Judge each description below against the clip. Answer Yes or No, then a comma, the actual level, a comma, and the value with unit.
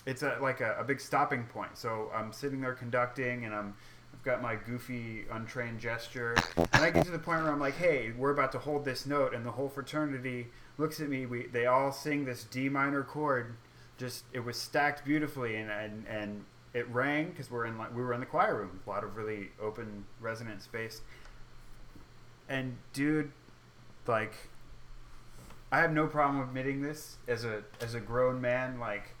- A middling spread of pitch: Yes, average, 3.5 semitones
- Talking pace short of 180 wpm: No, average, 195 wpm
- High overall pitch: No, low, 125 Hz